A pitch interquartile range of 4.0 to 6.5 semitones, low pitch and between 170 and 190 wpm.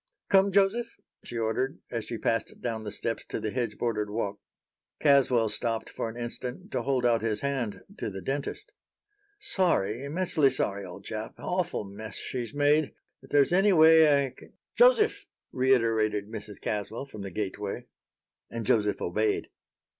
No: average, 5.0 semitones; low, 120 Hz; average, 160 wpm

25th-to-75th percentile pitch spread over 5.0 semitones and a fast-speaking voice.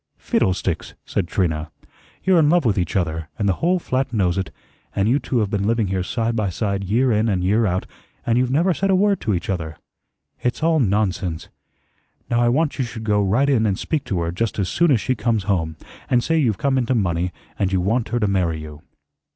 Yes: wide, 5.5 semitones; fast, 230 wpm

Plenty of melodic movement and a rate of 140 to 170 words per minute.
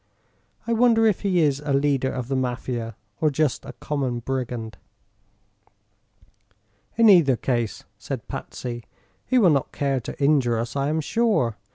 No: average, 4.4 semitones; average, 155 wpm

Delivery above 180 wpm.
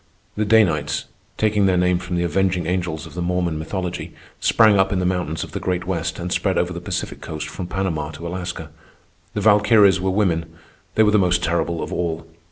Yes: fast, 205 wpm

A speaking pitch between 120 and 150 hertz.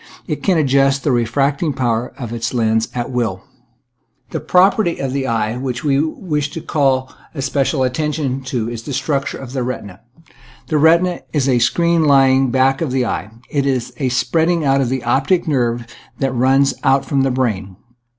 Yes: low, 135 Hz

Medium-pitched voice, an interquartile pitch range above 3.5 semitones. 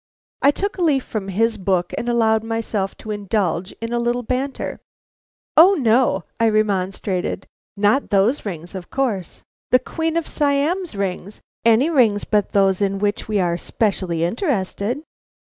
No: high, 220 Hz; average, 4.8 semitones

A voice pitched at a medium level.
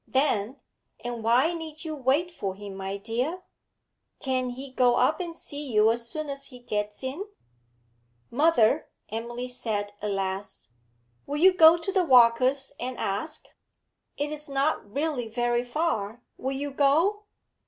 No: very high, 260 Hz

